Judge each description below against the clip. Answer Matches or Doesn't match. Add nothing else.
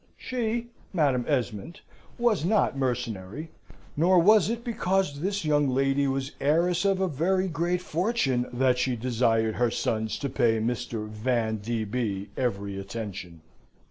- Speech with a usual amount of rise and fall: Doesn't match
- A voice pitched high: Doesn't match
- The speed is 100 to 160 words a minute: Matches